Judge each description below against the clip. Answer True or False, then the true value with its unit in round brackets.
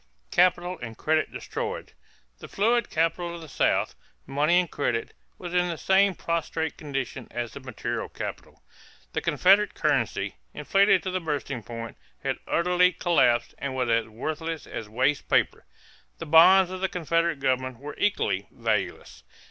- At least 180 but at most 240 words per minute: False (155 wpm)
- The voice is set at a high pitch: False (160 Hz)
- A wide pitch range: True (5.7 semitones)